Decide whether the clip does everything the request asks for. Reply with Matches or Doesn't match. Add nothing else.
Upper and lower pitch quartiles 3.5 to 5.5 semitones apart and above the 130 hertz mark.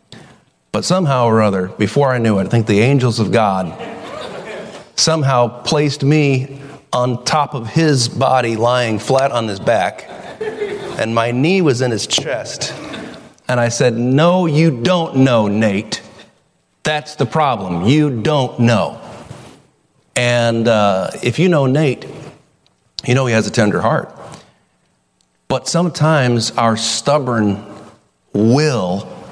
Doesn't match